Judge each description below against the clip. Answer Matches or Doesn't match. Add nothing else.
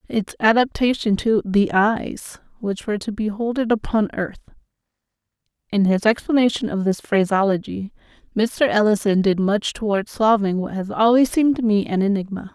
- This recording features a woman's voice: Matches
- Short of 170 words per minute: Matches